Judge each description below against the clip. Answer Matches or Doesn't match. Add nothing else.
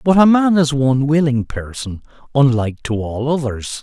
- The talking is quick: Doesn't match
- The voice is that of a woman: Doesn't match